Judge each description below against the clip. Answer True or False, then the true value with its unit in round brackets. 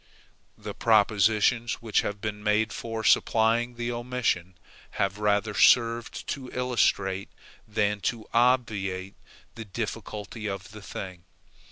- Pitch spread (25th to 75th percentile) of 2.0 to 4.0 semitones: True (2.5 semitones)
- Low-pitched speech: True (110 Hz)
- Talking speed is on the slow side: True (120 wpm)